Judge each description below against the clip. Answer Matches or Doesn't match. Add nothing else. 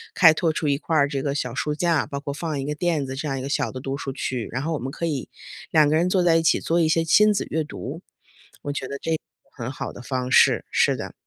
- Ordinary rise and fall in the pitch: Matches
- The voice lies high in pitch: Doesn't match